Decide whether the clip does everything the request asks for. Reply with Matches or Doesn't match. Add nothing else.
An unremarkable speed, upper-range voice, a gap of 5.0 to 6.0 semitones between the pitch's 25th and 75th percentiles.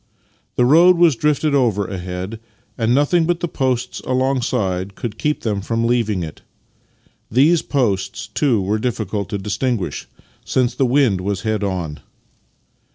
Doesn't match